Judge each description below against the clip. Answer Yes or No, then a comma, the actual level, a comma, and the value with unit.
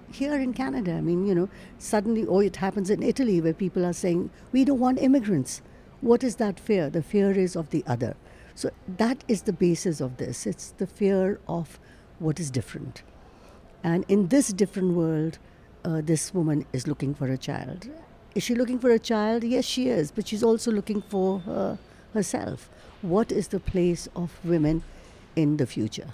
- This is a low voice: No, high, 195 Hz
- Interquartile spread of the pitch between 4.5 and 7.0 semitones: Yes, average, 5.2 semitones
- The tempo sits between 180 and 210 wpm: Yes, fast, 190 wpm